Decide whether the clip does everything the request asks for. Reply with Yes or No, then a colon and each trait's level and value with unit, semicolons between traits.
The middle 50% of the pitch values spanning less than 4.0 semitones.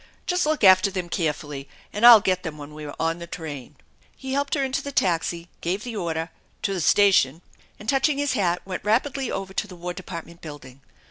No: wide, 5.5 semitones